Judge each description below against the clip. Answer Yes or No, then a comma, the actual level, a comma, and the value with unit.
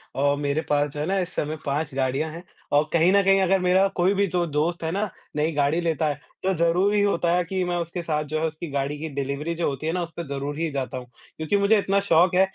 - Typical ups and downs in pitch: Yes, average, 3.7 semitones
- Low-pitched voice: No, medium, 165 Hz